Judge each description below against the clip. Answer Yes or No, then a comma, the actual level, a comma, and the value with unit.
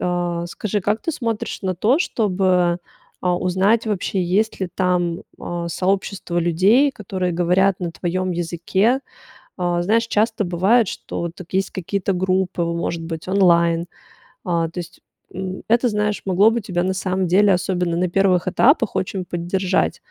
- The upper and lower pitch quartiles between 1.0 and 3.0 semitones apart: Yes, narrow, 2.5 semitones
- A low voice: No, medium, 185 Hz